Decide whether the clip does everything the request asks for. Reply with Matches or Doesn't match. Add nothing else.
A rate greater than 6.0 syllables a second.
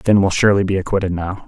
Matches